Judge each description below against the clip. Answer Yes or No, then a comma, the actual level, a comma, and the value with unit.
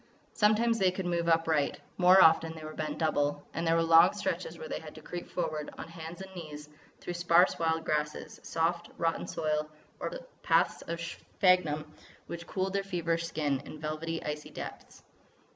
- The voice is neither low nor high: Yes, medium, 165 Hz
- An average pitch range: No, narrow, 2.2 semitones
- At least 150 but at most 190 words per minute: Yes, average, 175 wpm